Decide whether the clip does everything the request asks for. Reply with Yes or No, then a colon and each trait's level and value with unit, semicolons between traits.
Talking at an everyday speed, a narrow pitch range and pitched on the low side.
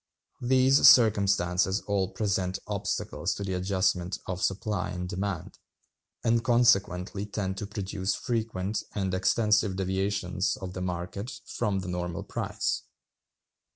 No: slow, 120 wpm; narrow, 2.3 semitones; very low, 95 Hz